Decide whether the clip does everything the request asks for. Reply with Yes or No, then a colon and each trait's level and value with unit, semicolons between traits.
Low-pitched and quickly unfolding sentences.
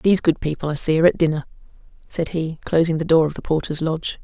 No: medium, 160 Hz; fast, 240 wpm